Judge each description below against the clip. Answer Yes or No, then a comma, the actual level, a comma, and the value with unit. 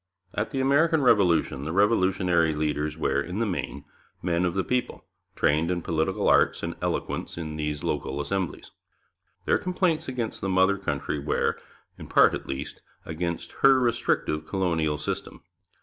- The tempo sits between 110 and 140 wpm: No, average, 155 wpm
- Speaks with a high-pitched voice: No, very low, 90 Hz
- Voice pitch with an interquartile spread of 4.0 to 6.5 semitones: Yes, average, 5.2 semitones